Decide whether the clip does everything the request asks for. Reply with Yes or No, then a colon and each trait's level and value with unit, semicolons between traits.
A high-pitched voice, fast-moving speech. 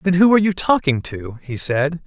No: medium, 160 Hz; fast, 230 wpm